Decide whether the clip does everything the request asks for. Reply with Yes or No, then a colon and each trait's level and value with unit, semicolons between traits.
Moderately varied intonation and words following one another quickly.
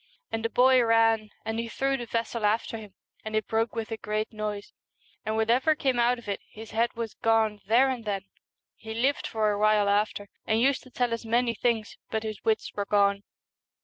No: narrow, 1.8 semitones; fast, 215 wpm